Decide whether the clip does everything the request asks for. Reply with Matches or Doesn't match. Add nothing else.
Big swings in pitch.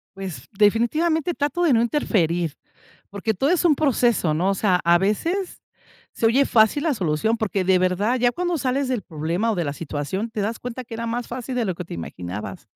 Matches